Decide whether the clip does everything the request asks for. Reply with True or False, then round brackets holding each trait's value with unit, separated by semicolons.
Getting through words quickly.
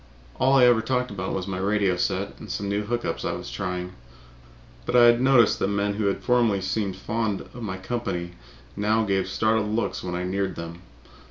True (220 wpm)